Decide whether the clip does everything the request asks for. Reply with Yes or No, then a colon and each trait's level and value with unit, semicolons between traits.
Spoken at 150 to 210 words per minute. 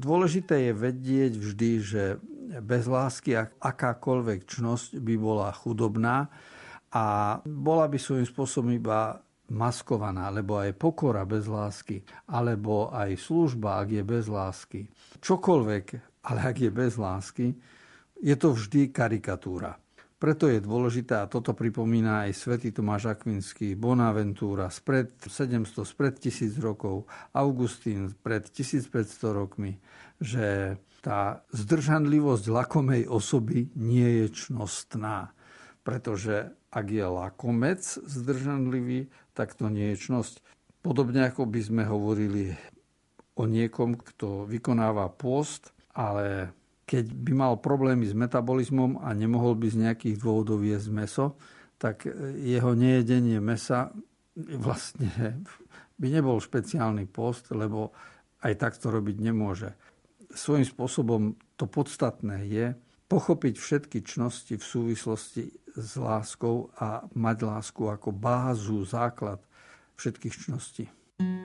No: average, 115 wpm